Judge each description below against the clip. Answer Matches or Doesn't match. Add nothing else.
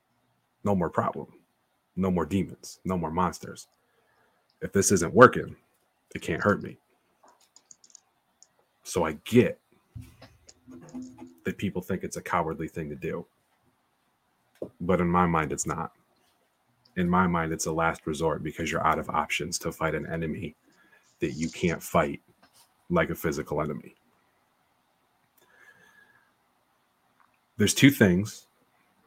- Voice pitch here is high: Doesn't match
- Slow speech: Matches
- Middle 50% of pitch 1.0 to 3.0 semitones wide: Matches